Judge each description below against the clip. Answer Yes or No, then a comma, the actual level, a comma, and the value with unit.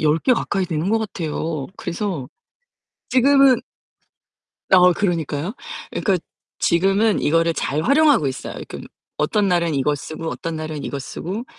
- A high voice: No, medium, 170 Hz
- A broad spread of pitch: No, average, 5.0 semitones